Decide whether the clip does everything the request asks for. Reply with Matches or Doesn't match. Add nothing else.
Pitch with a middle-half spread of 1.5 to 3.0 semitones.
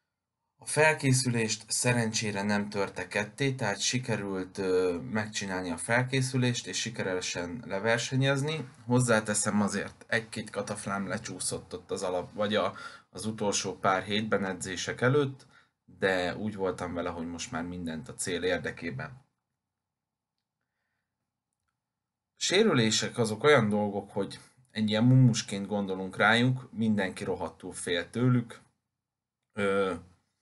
Doesn't match